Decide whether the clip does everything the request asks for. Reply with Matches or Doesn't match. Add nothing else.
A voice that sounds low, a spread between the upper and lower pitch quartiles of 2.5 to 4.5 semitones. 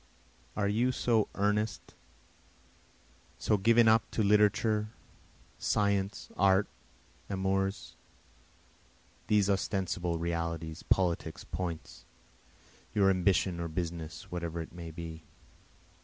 Matches